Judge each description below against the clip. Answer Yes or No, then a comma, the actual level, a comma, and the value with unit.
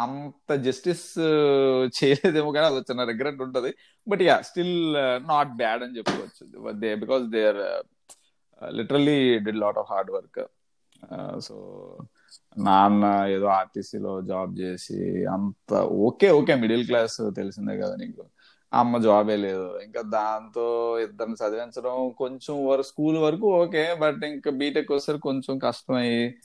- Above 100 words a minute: Yes, fast, 125 wpm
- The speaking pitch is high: No, low, 130 Hz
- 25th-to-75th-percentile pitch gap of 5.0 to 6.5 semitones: Yes, average, 5.3 semitones